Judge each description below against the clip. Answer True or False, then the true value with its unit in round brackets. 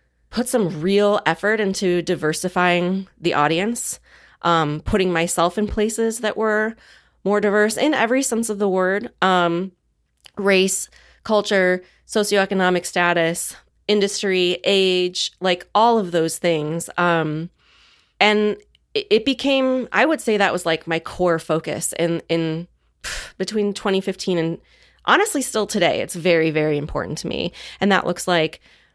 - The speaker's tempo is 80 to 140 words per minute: True (135 wpm)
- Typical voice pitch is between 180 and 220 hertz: True (185 Hz)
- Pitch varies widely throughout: False (3.7 semitones)